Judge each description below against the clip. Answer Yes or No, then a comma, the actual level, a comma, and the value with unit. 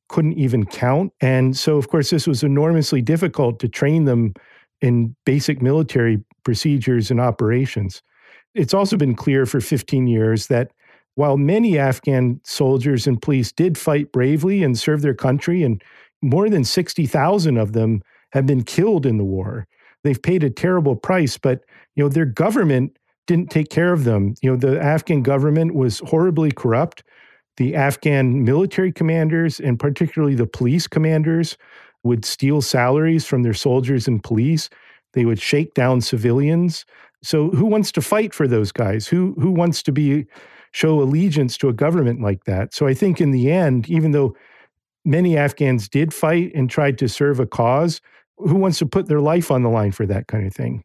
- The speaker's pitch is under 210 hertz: Yes, medium, 140 Hz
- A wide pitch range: No, average, 4.4 semitones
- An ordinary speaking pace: Yes, average, 180 wpm